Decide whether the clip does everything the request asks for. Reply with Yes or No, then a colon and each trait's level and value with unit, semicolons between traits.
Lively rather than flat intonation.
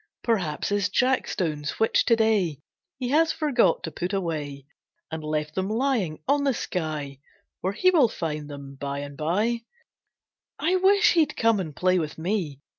Yes: wide, 7.8 semitones